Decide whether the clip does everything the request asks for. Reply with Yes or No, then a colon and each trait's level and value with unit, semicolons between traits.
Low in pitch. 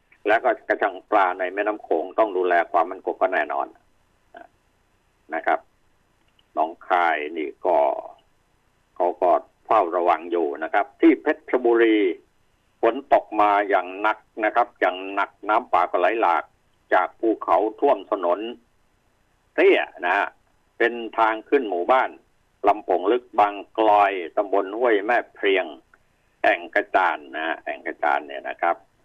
No: medium, 145 Hz